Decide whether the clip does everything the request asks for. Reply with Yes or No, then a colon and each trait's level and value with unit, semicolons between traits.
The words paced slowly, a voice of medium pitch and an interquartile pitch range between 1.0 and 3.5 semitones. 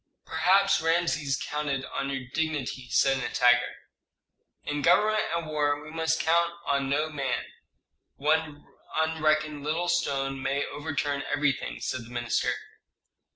Yes: slow, 125 wpm; medium, 145 Hz; average, 2.8 semitones